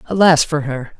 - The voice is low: No, medium, 150 Hz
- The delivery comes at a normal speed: Yes, average, 180 wpm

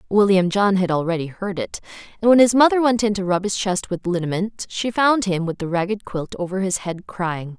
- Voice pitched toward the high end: Yes, high, 195 Hz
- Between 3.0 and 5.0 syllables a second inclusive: No, 5.4 syllables/s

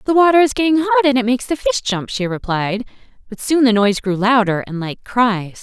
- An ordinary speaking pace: No, fast, 235 wpm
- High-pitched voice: Yes, high, 230 Hz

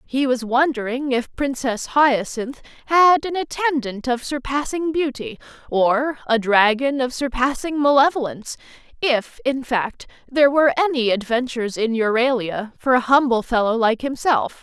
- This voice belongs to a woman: Yes, female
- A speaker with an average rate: No, slow, 130 wpm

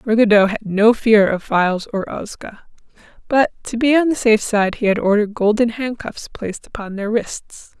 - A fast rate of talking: No, average, 185 wpm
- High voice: Yes, high, 220 Hz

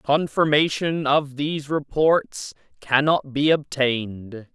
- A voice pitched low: No, medium, 145 Hz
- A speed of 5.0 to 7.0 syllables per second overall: No, 3.6 syllables/s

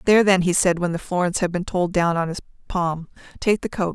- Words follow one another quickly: Yes, fast, 260 wpm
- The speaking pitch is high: No, medium, 180 Hz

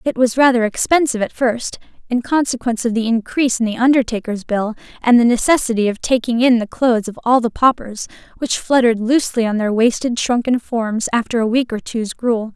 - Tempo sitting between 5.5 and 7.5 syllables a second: Yes, 5.8 syllables/s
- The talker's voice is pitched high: Yes, high, 235 Hz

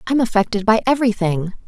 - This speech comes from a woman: Yes, female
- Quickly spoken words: No, average, 145 wpm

